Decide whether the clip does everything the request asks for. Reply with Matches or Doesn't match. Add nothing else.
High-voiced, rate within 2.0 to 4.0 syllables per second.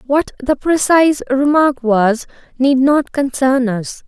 Matches